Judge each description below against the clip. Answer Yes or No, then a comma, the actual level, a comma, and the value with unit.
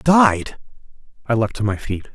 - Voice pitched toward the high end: No, low, 120 Hz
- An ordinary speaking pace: Yes, average, 170 wpm